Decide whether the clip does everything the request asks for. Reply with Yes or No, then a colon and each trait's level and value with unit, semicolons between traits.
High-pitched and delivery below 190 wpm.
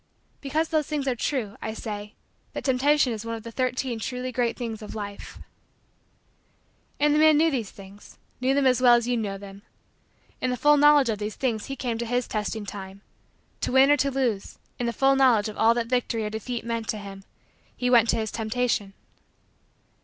No: high, 235 Hz; fast, 205 wpm